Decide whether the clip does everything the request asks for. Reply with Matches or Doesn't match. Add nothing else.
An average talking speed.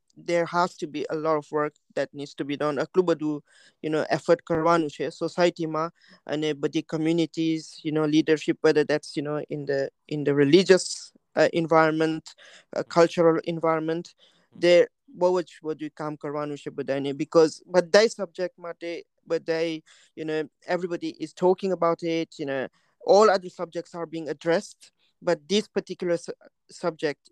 Doesn't match